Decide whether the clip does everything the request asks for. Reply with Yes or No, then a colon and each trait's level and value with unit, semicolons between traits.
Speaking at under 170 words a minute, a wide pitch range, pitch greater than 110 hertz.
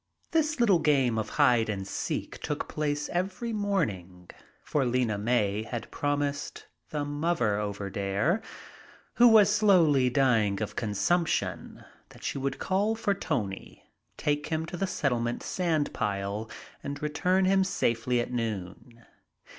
Yes: slow, 135 wpm; wide, 8.2 semitones; medium, 140 Hz